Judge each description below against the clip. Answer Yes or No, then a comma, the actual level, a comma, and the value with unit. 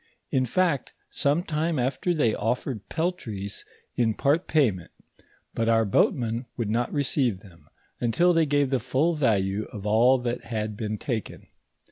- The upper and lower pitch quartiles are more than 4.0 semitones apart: Yes, average, 5.0 semitones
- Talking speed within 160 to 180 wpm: No, average, 150 wpm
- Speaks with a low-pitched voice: Yes, low, 125 Hz